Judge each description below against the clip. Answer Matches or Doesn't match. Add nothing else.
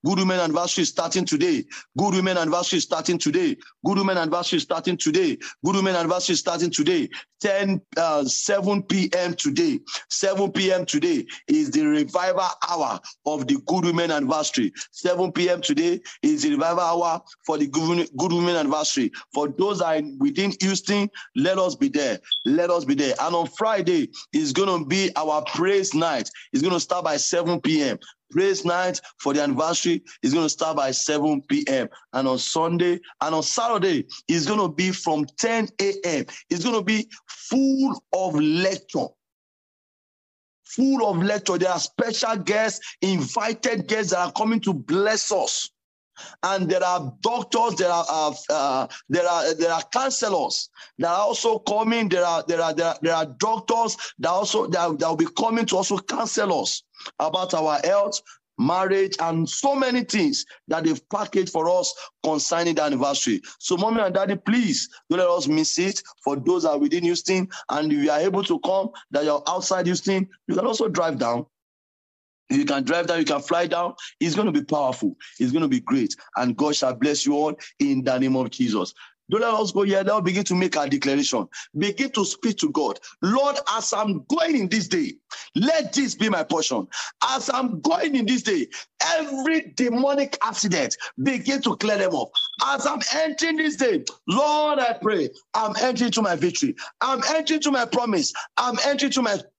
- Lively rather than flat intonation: Matches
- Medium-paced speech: Matches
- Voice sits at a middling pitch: Doesn't match